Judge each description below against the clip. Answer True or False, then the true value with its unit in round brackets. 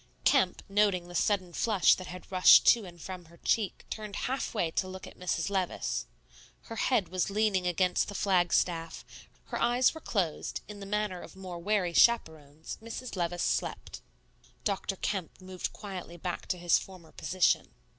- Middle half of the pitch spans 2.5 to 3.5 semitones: True (2.8 semitones)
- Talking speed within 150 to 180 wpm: True (170 wpm)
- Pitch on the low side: False (185 Hz)